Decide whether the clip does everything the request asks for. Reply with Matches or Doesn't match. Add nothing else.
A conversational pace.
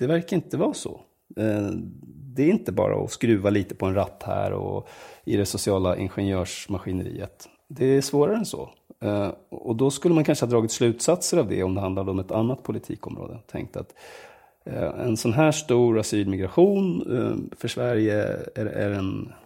Matches